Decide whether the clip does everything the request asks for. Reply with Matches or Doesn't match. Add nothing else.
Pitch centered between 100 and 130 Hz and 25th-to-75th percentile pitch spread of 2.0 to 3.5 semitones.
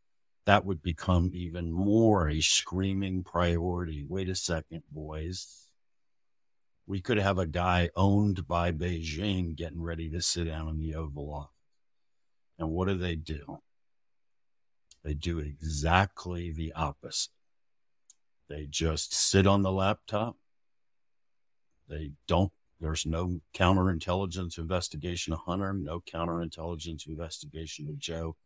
Doesn't match